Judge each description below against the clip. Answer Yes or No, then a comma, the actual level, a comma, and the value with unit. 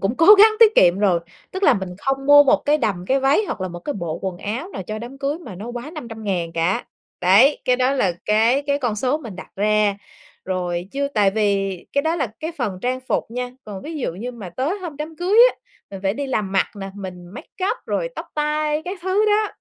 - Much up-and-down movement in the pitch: Yes, wide, 7.3 semitones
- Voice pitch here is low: No, high, 245 Hz